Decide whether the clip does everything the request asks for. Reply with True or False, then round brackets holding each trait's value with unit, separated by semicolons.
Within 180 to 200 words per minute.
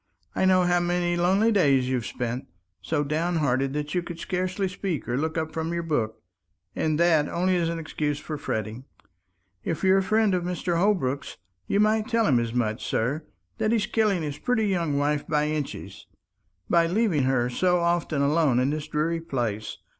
True (185 wpm)